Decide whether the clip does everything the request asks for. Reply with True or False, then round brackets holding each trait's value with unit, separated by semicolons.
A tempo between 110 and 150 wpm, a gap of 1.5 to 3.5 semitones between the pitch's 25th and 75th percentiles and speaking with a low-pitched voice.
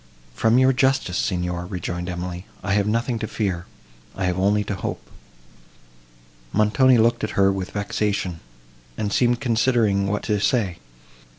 False (140 wpm; 4.0 semitones; 100 Hz)